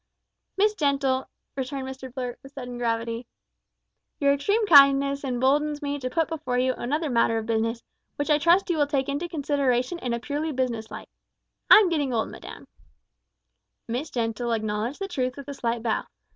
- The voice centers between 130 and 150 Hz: No, very high, 270 Hz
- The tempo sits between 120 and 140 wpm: No, average, 175 wpm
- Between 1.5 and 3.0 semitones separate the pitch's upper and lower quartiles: No, average, 3.4 semitones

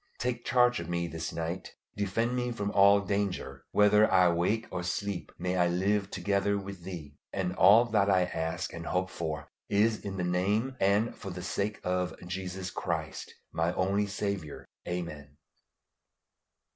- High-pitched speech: No, very low, 95 Hz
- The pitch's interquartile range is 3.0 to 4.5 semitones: No, narrow, 2.6 semitones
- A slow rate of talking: No, average, 160 wpm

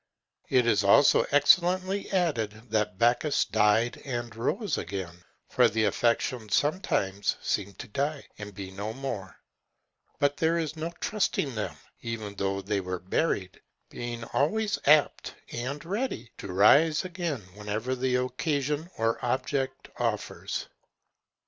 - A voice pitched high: No, low, 120 Hz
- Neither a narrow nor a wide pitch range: No, wide, 6.1 semitones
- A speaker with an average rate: No, slow, 130 wpm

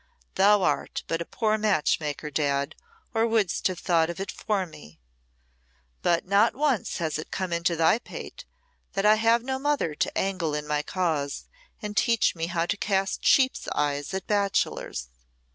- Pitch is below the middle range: No, medium, 185 Hz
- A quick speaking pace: No, average, 175 wpm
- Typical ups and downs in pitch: Yes, average, 5.0 semitones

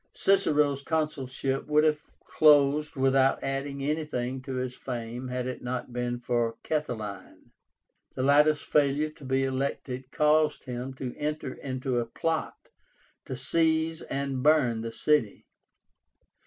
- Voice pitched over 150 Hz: No, low, 135 Hz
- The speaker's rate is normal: No, slow, 130 wpm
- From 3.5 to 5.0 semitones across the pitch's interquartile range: No, average, 3.1 semitones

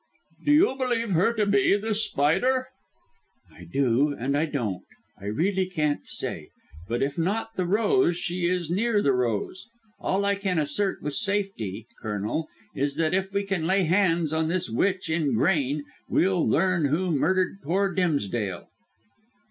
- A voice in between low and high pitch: Yes, medium, 175 Hz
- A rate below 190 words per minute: Yes, average, 160 wpm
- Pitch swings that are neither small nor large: No, wide, 5.7 semitones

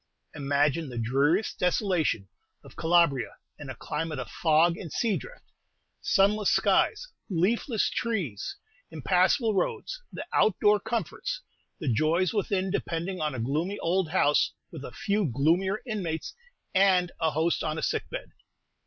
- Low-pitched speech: No, medium, 175 Hz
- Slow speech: No, average, 145 wpm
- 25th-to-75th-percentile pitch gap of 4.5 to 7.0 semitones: Yes, average, 4.8 semitones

